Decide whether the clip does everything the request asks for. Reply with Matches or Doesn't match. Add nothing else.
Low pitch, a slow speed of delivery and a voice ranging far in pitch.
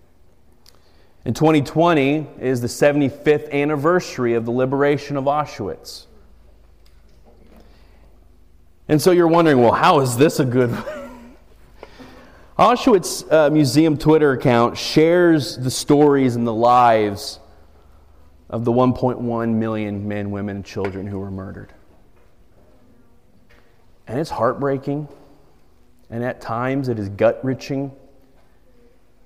Matches